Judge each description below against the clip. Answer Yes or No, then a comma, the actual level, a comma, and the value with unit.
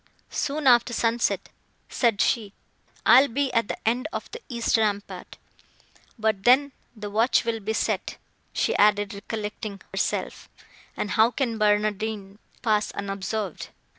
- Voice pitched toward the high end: Yes, high, 220 Hz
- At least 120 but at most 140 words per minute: Yes, slow, 135 wpm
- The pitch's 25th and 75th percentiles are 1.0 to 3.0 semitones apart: Yes, narrow, 2.5 semitones